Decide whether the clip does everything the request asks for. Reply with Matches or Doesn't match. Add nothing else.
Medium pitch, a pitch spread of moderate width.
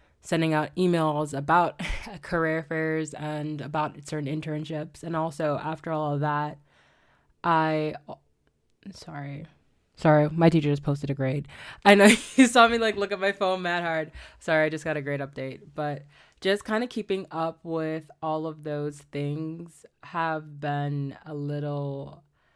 Doesn't match